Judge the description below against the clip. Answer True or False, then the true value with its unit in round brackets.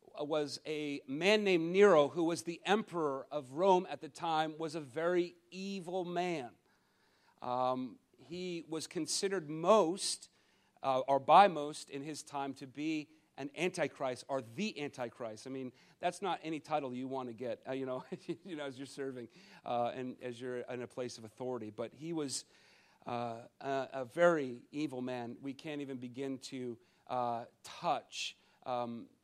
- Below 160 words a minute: False (165 wpm)